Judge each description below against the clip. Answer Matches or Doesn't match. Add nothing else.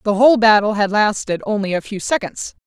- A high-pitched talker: Matches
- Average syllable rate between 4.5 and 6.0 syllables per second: Matches